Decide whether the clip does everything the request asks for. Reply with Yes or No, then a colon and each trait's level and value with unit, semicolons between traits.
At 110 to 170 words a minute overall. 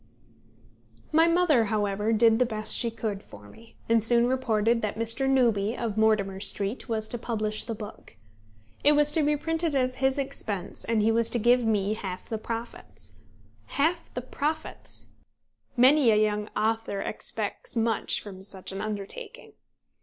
Yes: average, 160 wpm